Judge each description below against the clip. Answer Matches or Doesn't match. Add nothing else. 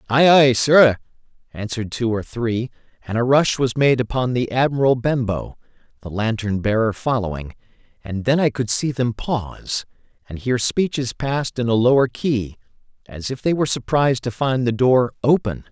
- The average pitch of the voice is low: Matches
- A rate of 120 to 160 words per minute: Doesn't match